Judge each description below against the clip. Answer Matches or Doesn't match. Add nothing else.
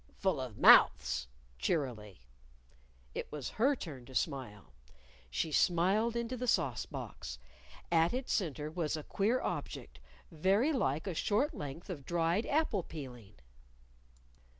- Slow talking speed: Matches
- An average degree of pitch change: Doesn't match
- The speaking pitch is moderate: Matches